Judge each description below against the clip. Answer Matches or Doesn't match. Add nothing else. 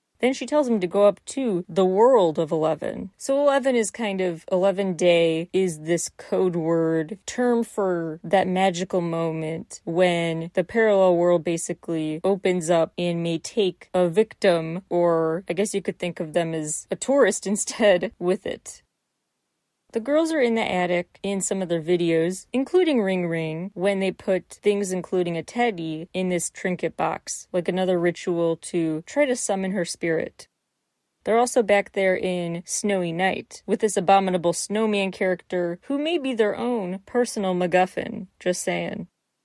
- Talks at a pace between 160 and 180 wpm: Matches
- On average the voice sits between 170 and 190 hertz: Matches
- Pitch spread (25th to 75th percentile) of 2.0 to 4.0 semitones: Matches